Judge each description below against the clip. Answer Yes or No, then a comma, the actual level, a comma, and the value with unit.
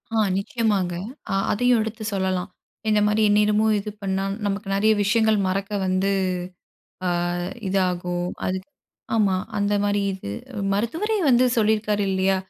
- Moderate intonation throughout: No, narrow, 2.3 semitones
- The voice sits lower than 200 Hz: No, high, 205 Hz